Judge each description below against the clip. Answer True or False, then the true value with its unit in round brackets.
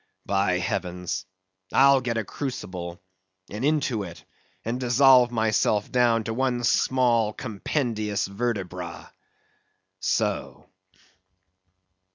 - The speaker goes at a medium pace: False (95 wpm)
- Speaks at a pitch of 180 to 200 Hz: False (115 Hz)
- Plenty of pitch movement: False (4.2 semitones)